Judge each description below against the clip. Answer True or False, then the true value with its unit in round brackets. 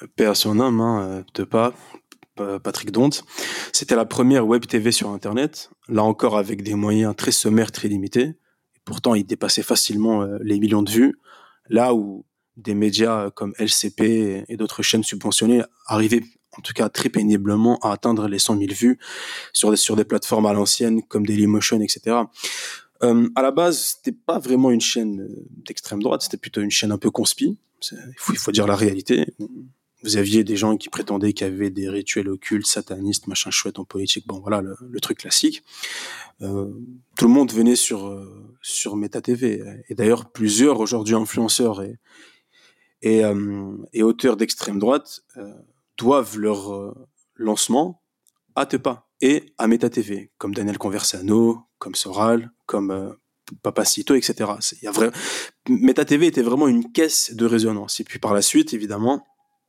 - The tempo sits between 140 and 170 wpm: True (165 wpm)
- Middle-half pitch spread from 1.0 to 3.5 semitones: True (2.7 semitones)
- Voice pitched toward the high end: False (110 Hz)